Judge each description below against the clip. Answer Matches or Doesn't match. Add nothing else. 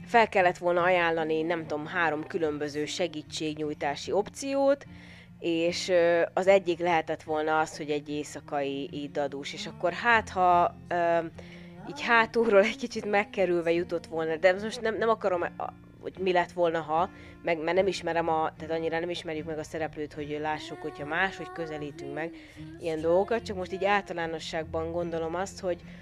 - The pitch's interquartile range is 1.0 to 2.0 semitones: Doesn't match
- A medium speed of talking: Doesn't match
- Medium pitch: Matches